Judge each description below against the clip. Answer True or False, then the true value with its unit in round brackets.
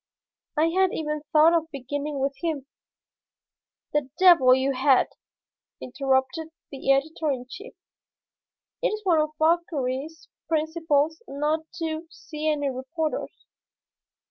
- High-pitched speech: True (305 Hz)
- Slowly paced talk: True (115 wpm)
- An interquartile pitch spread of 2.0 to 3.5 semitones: True (2.9 semitones)